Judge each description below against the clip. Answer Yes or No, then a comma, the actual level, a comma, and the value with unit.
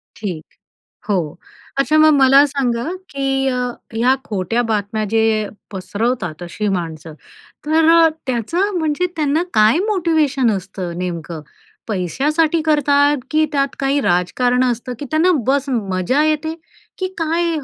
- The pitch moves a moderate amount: No, wide, 7.0 semitones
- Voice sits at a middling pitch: No, very high, 265 Hz